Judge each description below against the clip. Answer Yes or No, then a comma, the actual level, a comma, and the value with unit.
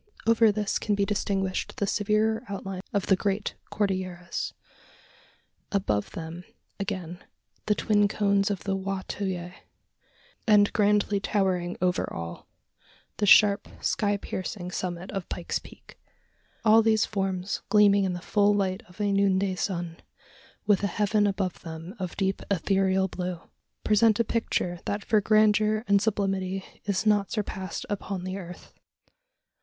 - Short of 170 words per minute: Yes, average, 145 wpm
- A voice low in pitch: No, high, 195 Hz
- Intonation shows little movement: Yes, narrow, 2.0 semitones